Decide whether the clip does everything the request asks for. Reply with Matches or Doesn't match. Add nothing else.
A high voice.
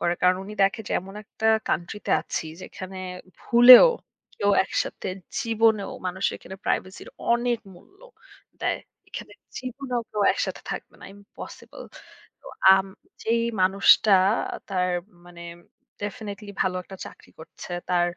Matches